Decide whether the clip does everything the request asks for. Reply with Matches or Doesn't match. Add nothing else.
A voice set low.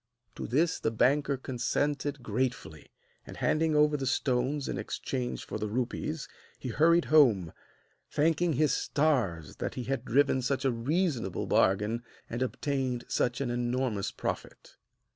Matches